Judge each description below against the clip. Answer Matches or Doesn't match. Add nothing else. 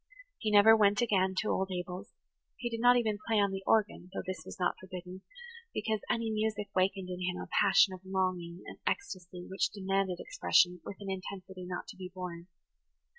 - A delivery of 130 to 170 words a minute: Doesn't match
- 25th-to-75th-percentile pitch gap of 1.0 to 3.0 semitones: Matches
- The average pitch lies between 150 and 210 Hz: Matches